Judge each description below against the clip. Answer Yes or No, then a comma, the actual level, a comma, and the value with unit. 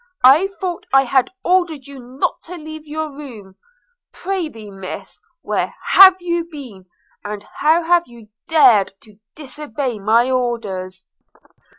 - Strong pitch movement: Yes, wide, 6.6 semitones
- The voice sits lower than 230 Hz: No, very high, 270 Hz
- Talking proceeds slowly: Yes, slow, 130 wpm